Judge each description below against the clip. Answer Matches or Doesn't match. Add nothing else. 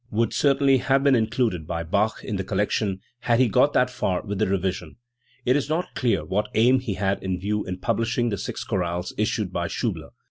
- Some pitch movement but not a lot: Matches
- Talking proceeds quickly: Matches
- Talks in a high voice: Doesn't match